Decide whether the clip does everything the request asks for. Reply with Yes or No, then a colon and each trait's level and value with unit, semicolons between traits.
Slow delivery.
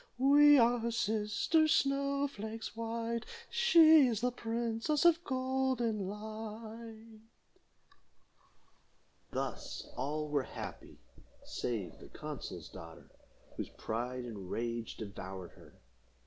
Yes: slow, 105 wpm